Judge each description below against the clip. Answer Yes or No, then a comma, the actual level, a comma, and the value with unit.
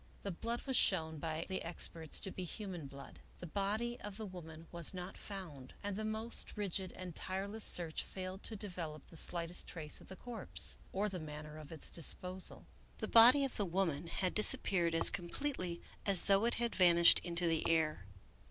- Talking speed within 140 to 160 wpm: No, average, 190 wpm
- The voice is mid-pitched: Yes, medium, 180 Hz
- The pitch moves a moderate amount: Yes, average, 3.7 semitones